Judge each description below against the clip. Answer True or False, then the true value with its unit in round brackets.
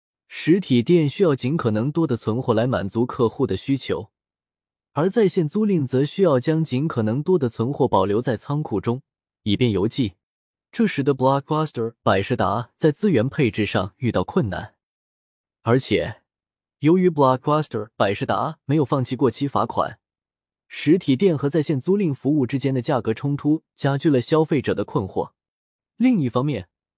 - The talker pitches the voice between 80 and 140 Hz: True (135 Hz)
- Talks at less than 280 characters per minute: False (285 characters per minute)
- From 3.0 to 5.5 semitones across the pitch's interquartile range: True (5.1 semitones)